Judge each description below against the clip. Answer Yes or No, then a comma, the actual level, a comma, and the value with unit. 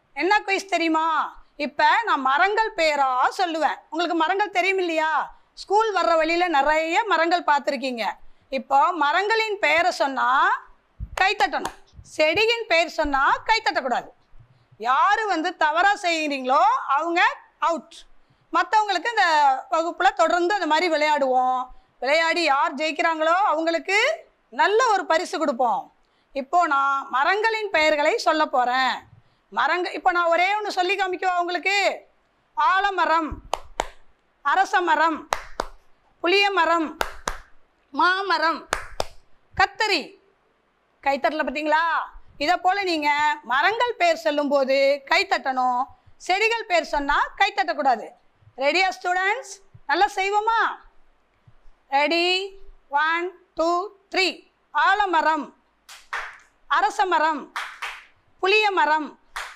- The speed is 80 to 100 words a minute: Yes, average, 90 wpm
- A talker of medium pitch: No, very high, 335 Hz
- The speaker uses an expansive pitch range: No, average, 4.0 semitones